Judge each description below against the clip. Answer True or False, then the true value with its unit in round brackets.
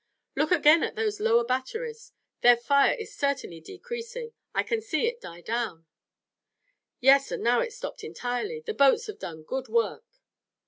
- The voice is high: True (390 Hz)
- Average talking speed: True (165 wpm)